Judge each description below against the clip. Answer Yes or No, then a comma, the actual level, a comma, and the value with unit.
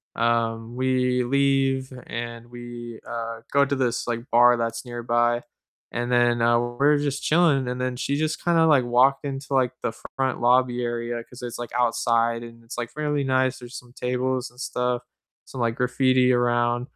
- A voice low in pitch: Yes, low, 125 Hz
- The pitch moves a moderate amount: No, narrow, 1.8 semitones